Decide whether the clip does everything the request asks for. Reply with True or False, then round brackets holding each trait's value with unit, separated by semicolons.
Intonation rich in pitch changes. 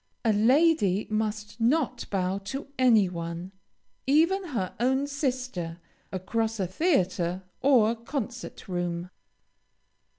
True (6.1 semitones)